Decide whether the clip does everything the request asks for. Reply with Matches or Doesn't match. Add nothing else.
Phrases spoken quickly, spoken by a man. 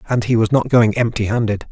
Matches